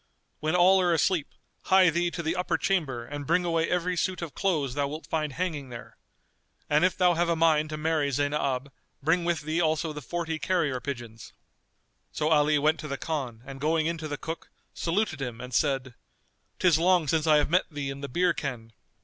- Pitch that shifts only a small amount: No, average, 3.4 semitones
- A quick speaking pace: Yes, fast, 210 wpm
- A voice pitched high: No, medium, 155 Hz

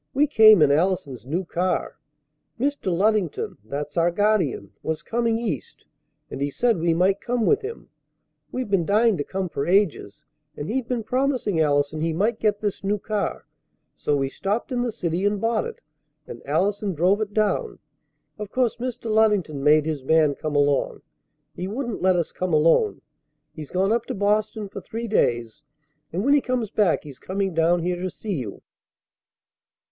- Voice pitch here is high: Yes, high, 195 Hz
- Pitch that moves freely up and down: Yes, wide, 5.7 semitones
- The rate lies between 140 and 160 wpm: No, average, 180 wpm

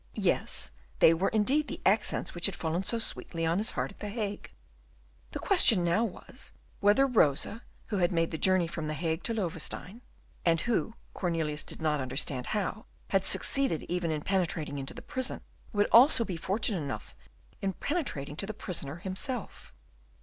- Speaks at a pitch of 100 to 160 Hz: No, medium, 185 Hz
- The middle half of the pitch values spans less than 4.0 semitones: No, average, 5.1 semitones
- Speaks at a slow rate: No, average, 175 wpm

